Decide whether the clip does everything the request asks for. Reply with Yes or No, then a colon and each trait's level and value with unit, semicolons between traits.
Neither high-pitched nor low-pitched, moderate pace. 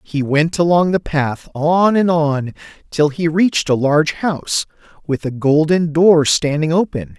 Yes: medium, 155 Hz; average, 165 wpm